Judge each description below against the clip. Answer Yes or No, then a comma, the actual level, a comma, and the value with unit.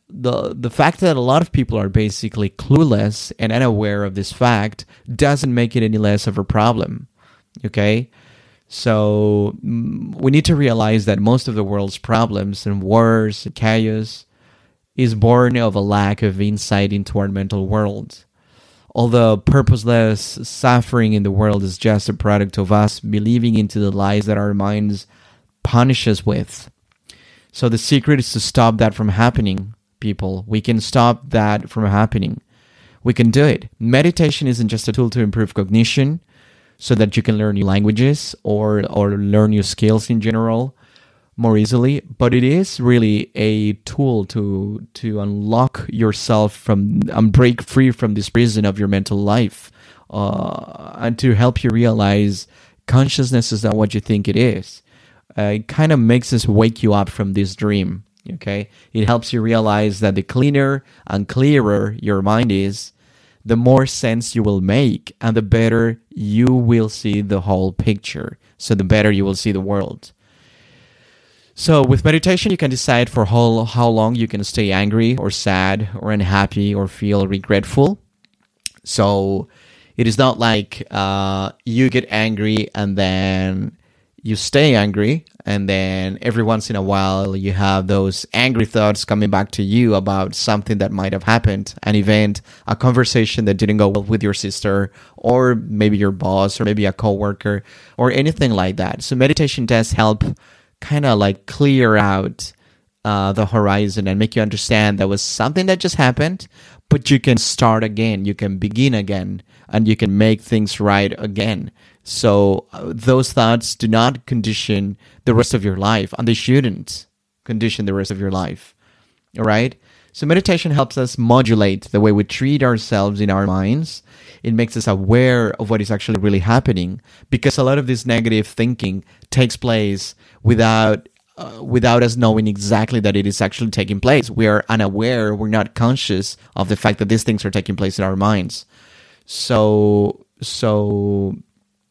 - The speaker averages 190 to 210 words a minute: No, average, 170 wpm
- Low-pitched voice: Yes, low, 110 Hz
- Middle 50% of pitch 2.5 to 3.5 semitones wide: Yes, average, 2.8 semitones